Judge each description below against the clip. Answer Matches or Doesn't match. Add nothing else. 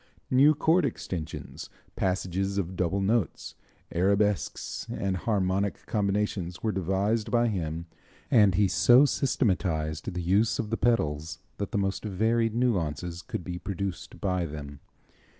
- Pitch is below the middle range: Matches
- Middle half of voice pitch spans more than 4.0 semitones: Doesn't match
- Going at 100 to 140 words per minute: Matches